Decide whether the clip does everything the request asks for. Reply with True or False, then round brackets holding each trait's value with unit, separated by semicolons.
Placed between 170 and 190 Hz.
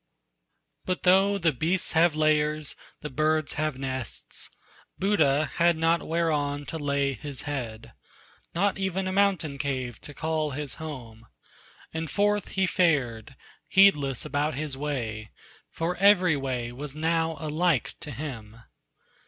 False (155 Hz)